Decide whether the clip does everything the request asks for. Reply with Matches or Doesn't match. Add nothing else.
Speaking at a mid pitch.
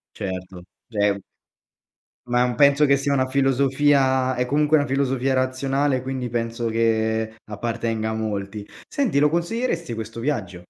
Doesn't match